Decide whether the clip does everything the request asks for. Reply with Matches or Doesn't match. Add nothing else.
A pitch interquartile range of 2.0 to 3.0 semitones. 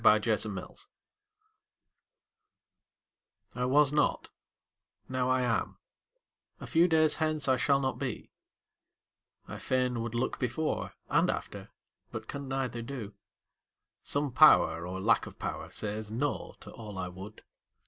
Doesn't match